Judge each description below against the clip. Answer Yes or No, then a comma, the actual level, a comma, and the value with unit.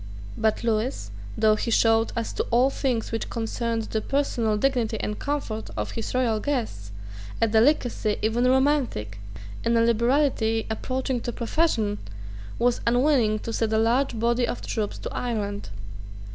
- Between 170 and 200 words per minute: No, average, 150 wpm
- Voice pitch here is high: Yes, high, 230 Hz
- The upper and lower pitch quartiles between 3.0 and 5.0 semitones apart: No, narrow, 2.4 semitones